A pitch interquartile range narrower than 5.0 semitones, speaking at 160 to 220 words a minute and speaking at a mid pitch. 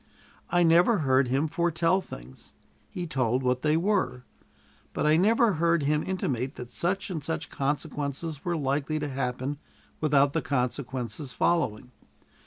No: average, 4.4 semitones; average, 145 wpm; medium, 150 Hz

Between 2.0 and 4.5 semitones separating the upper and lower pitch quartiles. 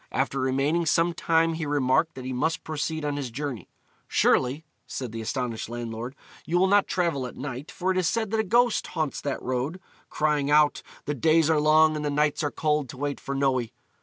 Yes: average, 3.7 semitones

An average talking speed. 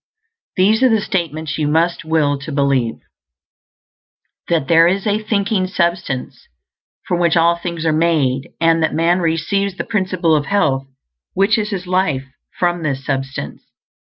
Yes: average, 155 wpm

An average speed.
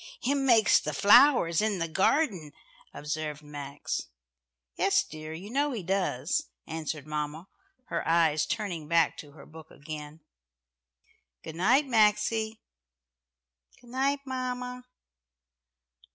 No: slow, 115 wpm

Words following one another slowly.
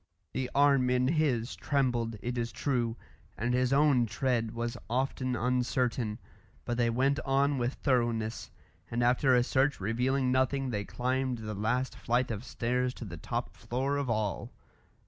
No: average, 160 wpm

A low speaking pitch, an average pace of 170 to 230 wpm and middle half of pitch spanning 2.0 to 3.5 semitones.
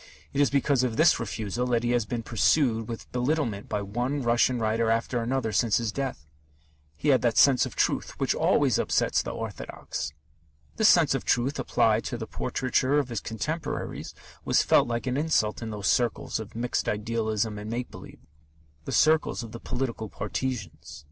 Yes: low, 120 Hz; average, 180 wpm; average, 3.0 semitones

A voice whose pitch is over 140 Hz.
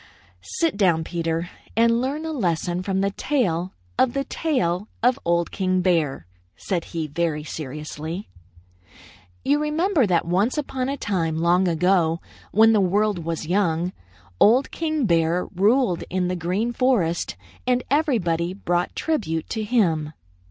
Yes: medium, 185 Hz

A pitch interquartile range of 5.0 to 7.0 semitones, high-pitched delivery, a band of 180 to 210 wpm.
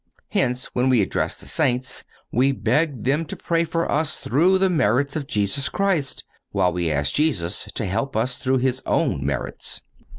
No: average, 5.3 semitones; low, 130 Hz; average, 185 wpm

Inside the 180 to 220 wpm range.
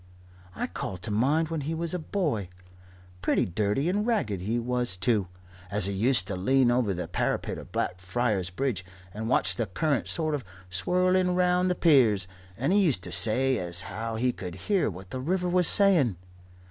Yes: average, 185 wpm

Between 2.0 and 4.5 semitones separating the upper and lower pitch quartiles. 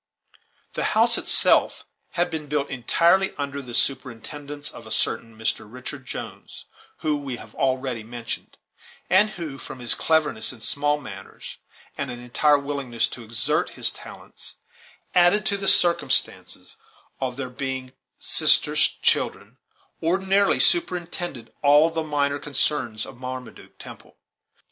Yes: average, 4.1 semitones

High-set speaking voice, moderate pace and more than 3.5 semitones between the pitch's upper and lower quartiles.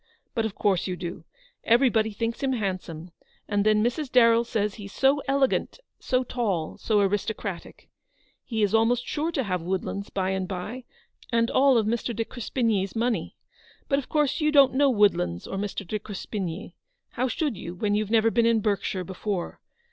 Yes: high, 220 Hz; average, 180 wpm; average, 3.9 semitones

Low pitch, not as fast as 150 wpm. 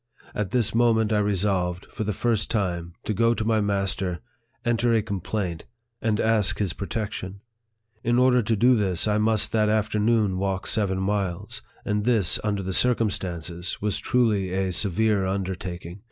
No: low, 105 Hz; average, 160 wpm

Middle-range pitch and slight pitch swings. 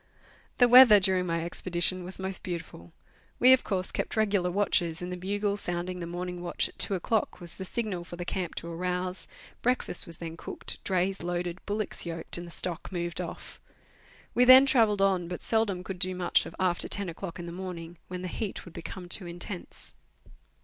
Yes: medium, 180 Hz; narrow, 2.2 semitones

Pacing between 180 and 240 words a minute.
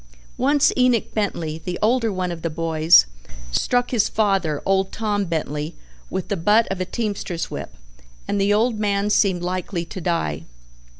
No: average, 165 wpm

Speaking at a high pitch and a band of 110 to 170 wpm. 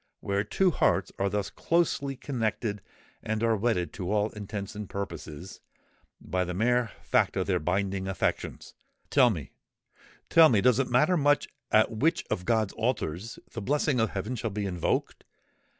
No: low, 110 Hz; average, 160 wpm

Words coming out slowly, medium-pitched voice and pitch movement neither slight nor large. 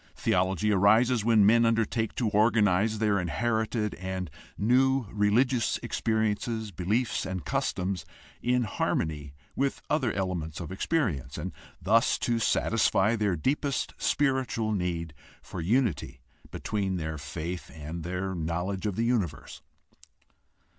No: slow, 120 wpm; low, 105 Hz; average, 4.4 semitones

